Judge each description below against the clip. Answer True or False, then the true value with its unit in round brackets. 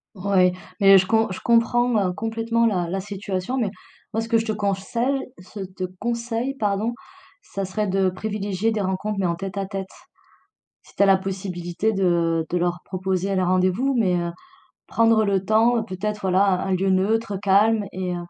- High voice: True (195 Hz)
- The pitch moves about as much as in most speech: True (3.0 semitones)